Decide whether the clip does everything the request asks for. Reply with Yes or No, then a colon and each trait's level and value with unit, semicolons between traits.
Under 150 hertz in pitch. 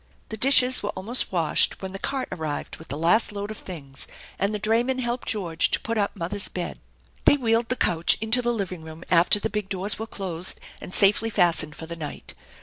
No: high, 200 Hz